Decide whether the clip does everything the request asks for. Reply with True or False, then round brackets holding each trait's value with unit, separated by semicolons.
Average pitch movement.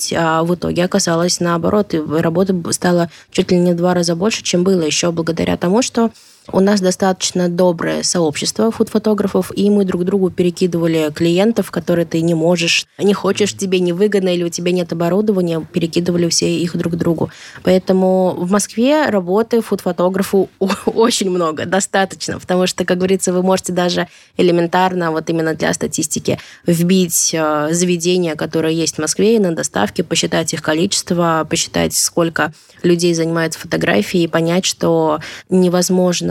False (2.3 semitones)